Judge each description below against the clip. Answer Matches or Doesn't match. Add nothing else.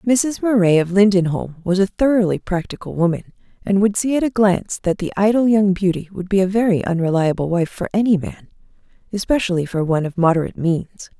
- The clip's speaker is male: Doesn't match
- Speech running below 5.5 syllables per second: Doesn't match